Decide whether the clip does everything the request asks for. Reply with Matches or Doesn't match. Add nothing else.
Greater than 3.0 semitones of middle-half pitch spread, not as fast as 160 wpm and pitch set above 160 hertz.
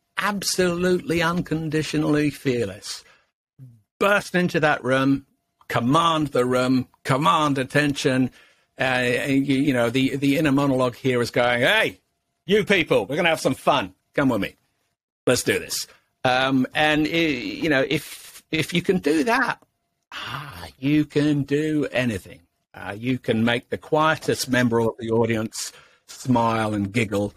Doesn't match